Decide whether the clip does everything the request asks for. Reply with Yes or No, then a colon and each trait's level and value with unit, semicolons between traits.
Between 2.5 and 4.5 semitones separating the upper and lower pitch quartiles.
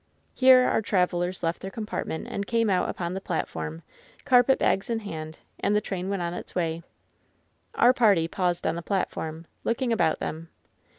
No: average, 4.9 semitones